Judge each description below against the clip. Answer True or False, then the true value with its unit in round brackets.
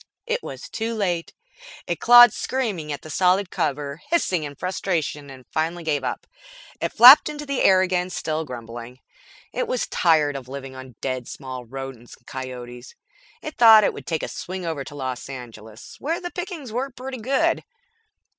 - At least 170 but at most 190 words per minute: True (175 wpm)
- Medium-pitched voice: True (160 Hz)